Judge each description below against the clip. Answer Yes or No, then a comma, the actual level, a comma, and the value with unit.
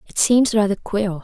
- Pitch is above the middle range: Yes, high, 205 Hz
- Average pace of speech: Yes, average, 195 wpm